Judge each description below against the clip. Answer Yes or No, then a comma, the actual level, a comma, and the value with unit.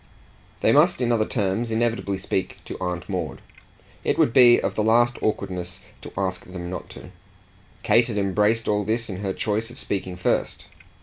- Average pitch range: Yes, average, 3.7 semitones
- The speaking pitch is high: No, low, 105 Hz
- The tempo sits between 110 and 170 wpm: No, average, 180 wpm